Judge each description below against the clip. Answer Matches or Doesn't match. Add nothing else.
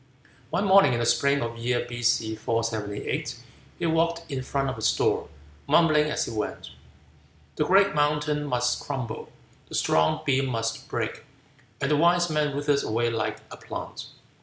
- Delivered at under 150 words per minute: Doesn't match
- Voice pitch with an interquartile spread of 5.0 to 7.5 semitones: Doesn't match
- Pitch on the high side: Doesn't match